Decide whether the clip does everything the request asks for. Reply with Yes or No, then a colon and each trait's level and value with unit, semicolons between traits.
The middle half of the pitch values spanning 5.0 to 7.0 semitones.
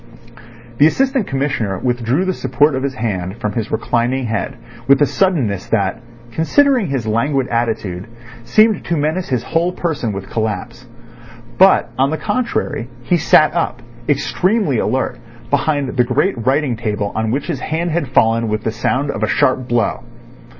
Yes: wide, 5.6 semitones